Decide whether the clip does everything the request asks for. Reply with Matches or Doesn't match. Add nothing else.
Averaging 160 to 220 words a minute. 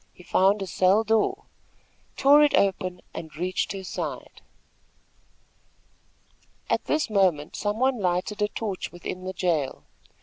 Doesn't match